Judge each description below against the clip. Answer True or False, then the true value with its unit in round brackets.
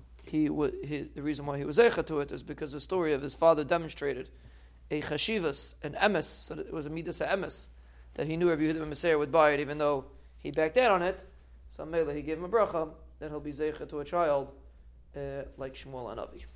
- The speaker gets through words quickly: True (240 wpm)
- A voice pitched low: False (150 Hz)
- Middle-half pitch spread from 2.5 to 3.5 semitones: True (3.0 semitones)